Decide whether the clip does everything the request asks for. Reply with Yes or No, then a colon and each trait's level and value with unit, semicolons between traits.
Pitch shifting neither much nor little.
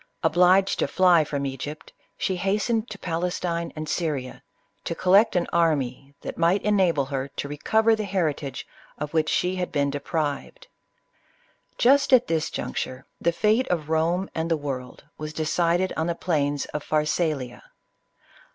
Yes: average, 4.0 semitones